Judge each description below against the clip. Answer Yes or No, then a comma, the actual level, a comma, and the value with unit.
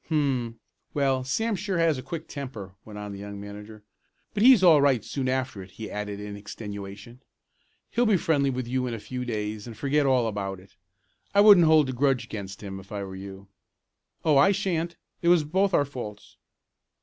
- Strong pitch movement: Yes, wide, 6.7 semitones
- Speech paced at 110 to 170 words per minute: No, average, 200 wpm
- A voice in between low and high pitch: No, low, 125 Hz